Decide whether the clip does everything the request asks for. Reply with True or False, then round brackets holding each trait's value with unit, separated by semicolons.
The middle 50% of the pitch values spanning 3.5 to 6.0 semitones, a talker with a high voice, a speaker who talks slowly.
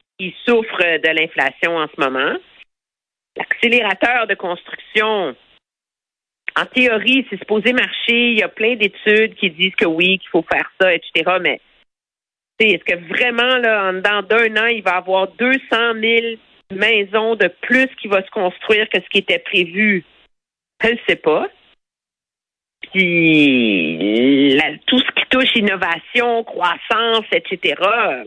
True (4.3 semitones; 210 Hz; 140 wpm)